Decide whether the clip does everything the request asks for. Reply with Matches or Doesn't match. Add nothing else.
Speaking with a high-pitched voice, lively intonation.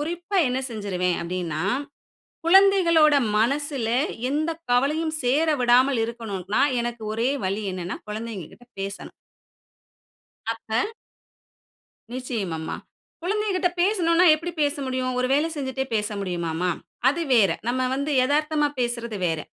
Matches